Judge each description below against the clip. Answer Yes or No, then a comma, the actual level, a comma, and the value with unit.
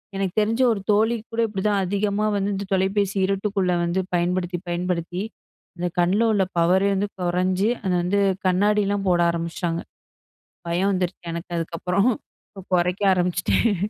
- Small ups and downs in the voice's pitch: Yes, narrow, 2.3 semitones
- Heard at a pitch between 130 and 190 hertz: Yes, medium, 185 Hz